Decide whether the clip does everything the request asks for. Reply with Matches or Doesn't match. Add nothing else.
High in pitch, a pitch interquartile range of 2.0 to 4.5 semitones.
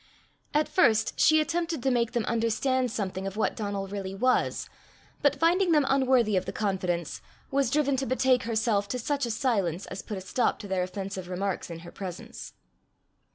Doesn't match